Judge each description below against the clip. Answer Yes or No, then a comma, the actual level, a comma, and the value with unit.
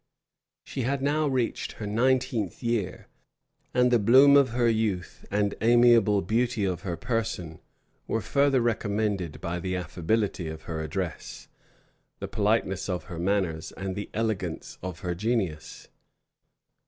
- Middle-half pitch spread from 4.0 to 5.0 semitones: Yes, average, 4.7 semitones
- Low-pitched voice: Yes, low, 105 Hz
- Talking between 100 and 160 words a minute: Yes, average, 140 wpm